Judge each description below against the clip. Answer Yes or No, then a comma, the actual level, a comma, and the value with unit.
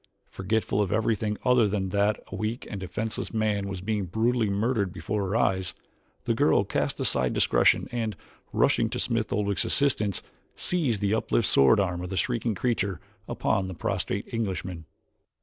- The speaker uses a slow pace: No, average, 165 wpm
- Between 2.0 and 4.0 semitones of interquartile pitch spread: Yes, average, 2.7 semitones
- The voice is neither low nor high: No, low, 105 Hz